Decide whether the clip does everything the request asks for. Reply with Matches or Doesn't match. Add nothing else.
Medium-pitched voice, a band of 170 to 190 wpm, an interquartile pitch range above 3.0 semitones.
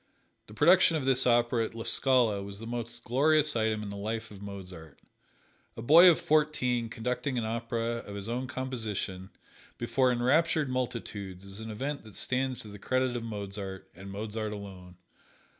Doesn't match